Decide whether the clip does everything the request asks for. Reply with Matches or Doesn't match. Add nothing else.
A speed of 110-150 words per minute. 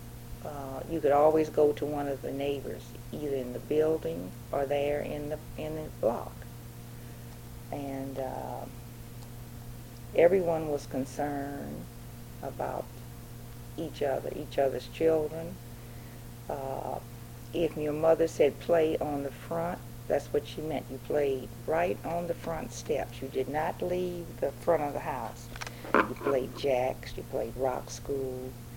Matches